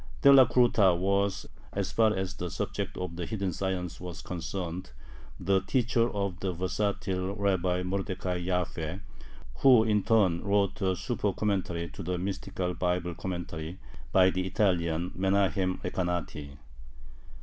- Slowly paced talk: Yes, slow, 125 wpm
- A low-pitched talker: Yes, very low, 95 Hz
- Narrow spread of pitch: Yes, narrow, 1.9 semitones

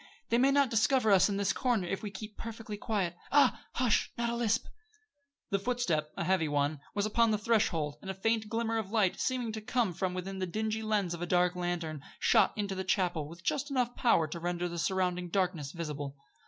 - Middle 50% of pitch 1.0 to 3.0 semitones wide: No, average, 4.3 semitones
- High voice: Yes, high, 195 Hz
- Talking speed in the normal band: No, fast, 210 wpm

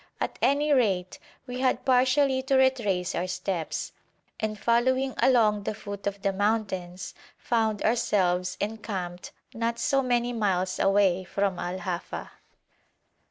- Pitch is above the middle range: Yes, high, 210 Hz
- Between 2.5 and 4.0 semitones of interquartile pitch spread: No, average, 4.8 semitones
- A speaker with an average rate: No, slow, 130 wpm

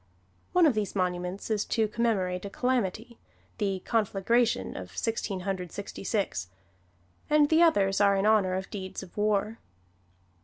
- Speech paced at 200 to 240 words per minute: No, average, 150 wpm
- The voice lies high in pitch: Yes, high, 200 Hz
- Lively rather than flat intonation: No, average, 3.2 semitones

